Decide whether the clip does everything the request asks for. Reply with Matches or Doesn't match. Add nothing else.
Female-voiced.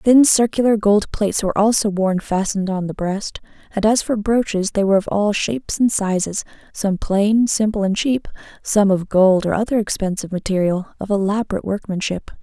Matches